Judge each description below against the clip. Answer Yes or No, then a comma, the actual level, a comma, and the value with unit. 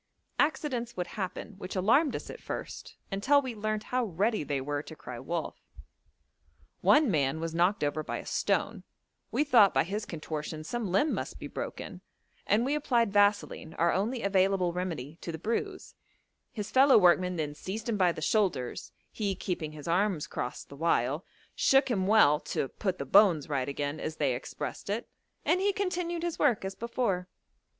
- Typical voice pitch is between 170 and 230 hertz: Yes, high, 190 Hz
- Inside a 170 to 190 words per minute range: Yes, average, 180 wpm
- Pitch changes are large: Yes, wide, 6.8 semitones